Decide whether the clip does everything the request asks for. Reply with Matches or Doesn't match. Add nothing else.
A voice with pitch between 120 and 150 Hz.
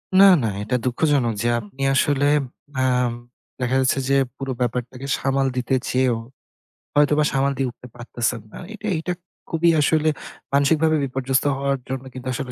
Matches